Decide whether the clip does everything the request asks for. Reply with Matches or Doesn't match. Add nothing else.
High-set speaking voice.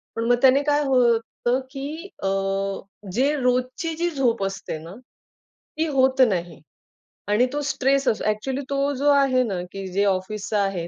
Matches